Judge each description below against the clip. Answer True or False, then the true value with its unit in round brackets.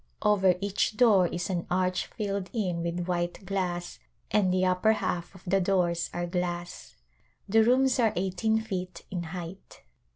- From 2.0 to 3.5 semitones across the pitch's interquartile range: True (2.4 semitones)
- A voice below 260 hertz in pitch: True (185 Hz)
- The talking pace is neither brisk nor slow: True (160 wpm)